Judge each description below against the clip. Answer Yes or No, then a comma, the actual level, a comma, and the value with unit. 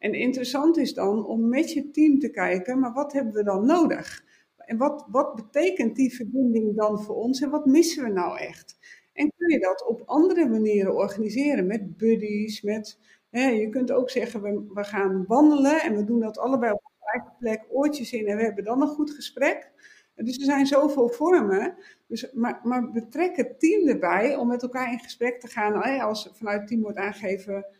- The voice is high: Yes, high, 245 Hz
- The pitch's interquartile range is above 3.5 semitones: Yes, average, 4.9 semitones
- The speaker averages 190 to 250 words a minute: Yes, fast, 200 wpm